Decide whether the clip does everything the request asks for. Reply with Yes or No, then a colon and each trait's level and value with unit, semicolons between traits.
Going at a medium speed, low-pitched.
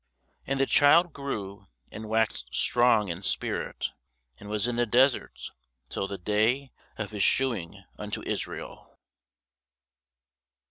No: slow, 125 wpm; low, 110 Hz